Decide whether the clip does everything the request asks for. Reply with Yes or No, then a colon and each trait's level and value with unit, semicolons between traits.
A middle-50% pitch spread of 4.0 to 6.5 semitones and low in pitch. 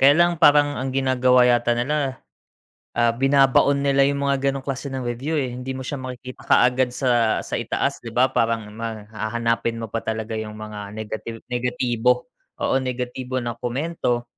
No: average, 2.7 semitones; low, 125 Hz